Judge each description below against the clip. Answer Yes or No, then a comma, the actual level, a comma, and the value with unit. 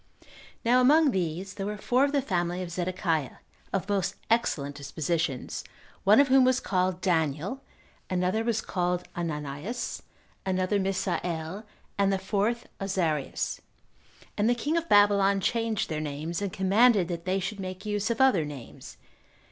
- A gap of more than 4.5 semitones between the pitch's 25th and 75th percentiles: No, average, 4.1 semitones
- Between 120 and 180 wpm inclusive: Yes, average, 150 wpm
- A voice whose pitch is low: No, high, 190 Hz